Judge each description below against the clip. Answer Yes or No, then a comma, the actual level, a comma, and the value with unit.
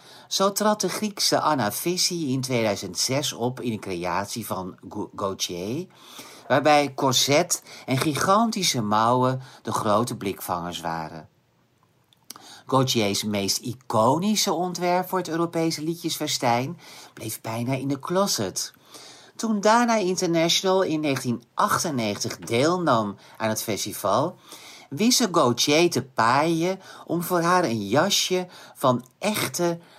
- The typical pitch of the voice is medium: Yes, medium, 145 Hz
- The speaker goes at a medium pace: No, slow, 115 wpm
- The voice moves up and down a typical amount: No, wide, 7.3 semitones